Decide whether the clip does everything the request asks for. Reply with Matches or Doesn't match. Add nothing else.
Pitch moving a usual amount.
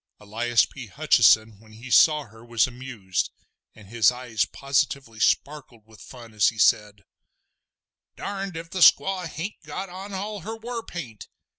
Doesn't match